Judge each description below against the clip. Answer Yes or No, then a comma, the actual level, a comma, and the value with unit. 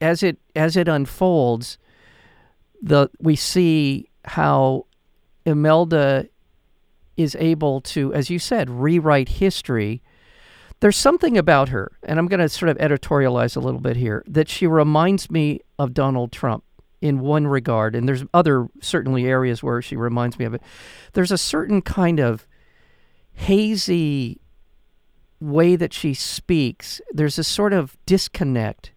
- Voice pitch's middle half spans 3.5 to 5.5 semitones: Yes, average, 5.2 semitones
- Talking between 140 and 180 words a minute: Yes, average, 145 wpm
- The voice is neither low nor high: Yes, medium, 145 Hz